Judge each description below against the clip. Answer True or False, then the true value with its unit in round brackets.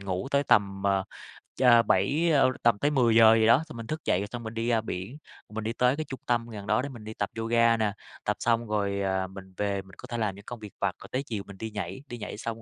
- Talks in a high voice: False (110 Hz)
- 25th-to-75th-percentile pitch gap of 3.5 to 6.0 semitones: False (3.0 semitones)